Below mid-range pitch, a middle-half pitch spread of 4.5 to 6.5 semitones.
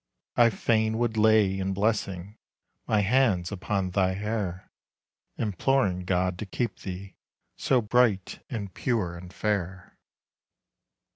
No: low, 100 Hz; average, 3.2 semitones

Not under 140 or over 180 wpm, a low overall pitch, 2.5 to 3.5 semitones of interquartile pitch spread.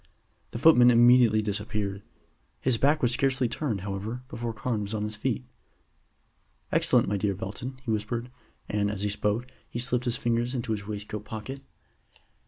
Yes: average, 165 wpm; low, 115 Hz; average, 2.9 semitones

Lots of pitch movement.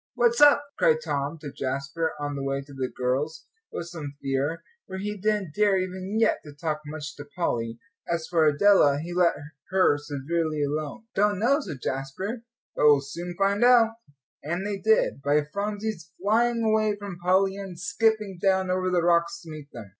Yes: wide, 5.8 semitones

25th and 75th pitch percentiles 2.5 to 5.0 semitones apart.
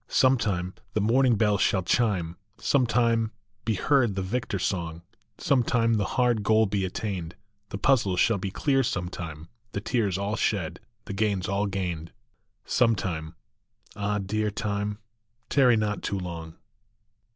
Yes: average, 3.6 semitones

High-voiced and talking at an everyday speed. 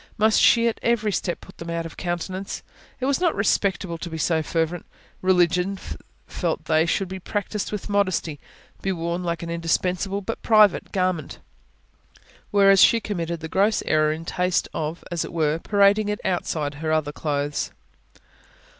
No: medium, 180 Hz; average, 165 wpm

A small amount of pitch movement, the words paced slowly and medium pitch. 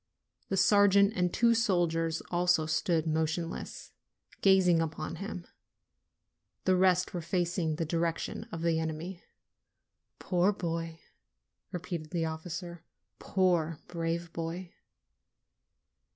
Yes: narrow, 2.0 semitones; slow, 105 wpm; medium, 170 Hz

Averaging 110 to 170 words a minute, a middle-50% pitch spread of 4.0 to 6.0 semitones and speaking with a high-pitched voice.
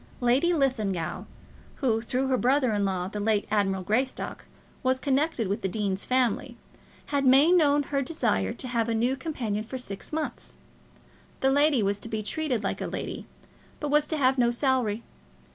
No: average, 180 wpm; average, 4.7 semitones; very high, 250 Hz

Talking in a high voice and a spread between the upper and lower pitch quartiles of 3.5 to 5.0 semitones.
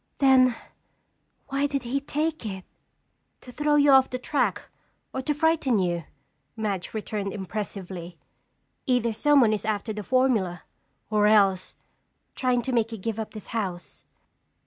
Yes: high, 225 Hz; average, 4.7 semitones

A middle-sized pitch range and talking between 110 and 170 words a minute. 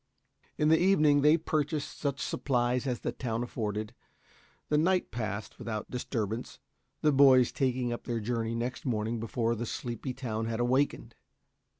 Yes: average, 3.5 semitones; average, 160 wpm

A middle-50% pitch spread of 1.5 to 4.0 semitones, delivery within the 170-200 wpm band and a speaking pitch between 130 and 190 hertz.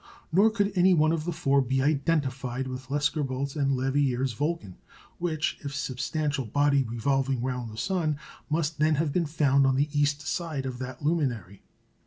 Yes: average, 3.0 semitones; average, 175 wpm; medium, 140 Hz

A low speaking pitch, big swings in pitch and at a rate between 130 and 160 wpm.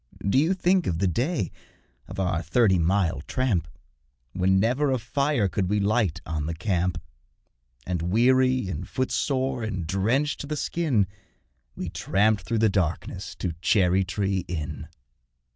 Yes: low, 100 Hz; wide, 6.1 semitones; average, 150 wpm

